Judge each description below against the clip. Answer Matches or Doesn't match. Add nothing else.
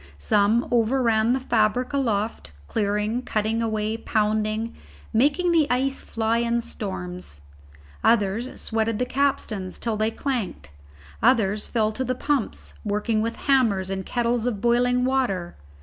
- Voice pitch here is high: Matches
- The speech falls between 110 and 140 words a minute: Matches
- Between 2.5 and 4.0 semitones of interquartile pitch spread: Matches